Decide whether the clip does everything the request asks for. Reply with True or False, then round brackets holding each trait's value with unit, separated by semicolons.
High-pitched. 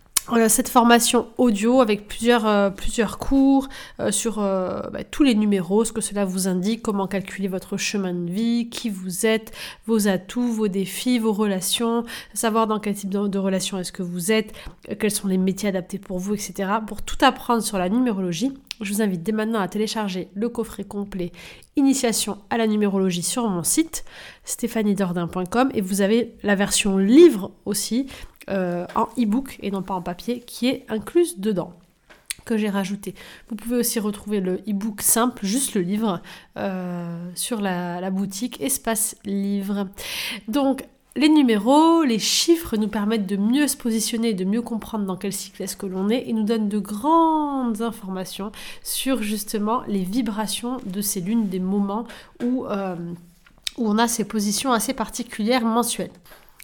True (215 Hz)